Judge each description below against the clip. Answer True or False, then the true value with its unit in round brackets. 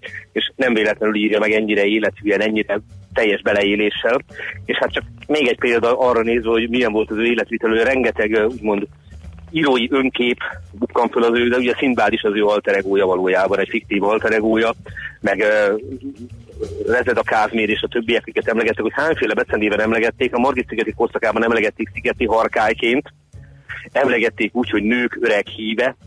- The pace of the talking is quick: True (160 wpm)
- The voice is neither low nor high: False (110 Hz)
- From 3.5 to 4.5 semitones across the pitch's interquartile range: False (2.8 semitones)